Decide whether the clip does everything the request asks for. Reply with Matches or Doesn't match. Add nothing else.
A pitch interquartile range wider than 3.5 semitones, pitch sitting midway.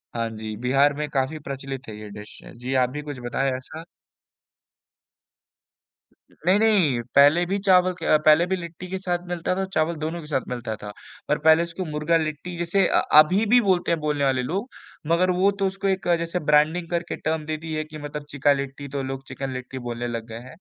Matches